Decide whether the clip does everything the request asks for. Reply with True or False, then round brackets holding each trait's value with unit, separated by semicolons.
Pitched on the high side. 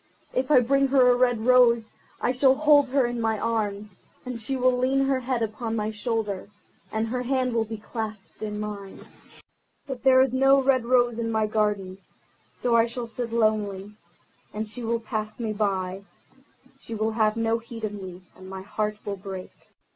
True (225 Hz)